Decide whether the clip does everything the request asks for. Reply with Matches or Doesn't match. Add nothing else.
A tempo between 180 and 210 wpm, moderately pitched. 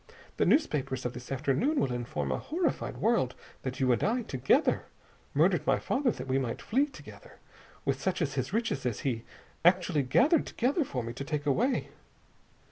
Matches